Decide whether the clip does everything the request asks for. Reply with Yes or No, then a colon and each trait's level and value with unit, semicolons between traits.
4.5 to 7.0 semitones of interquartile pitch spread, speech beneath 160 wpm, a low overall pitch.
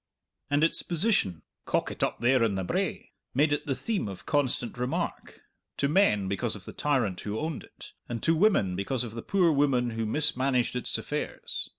No: average, 5.2 semitones; average, 190 wpm; low, 125 Hz